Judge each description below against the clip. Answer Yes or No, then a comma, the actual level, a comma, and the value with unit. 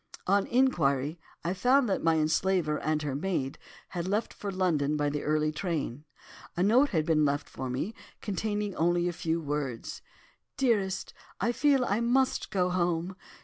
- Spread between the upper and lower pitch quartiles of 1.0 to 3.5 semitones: No, average, 5.0 semitones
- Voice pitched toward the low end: No, medium, 175 Hz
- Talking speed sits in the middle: Yes, average, 165 wpm